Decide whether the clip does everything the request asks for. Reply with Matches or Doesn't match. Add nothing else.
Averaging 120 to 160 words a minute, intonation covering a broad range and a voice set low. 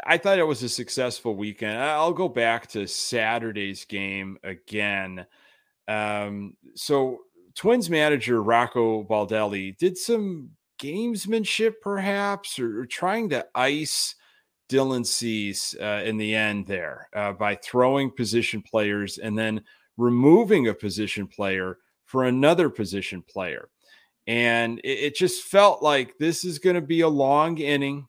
Matches